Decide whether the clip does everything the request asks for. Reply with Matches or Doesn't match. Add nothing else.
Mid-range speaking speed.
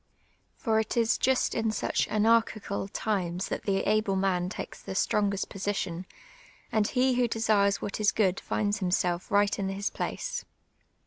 Matches